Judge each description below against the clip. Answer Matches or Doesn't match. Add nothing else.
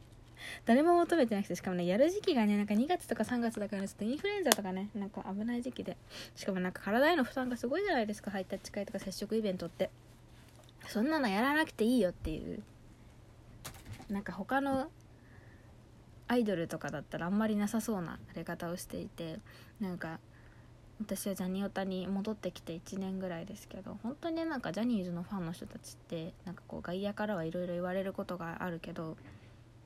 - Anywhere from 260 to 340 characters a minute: Doesn't match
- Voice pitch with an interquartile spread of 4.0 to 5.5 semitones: Matches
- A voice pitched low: Doesn't match